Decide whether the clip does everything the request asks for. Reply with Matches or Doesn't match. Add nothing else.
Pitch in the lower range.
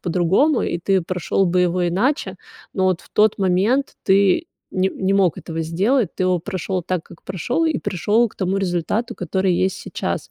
Doesn't match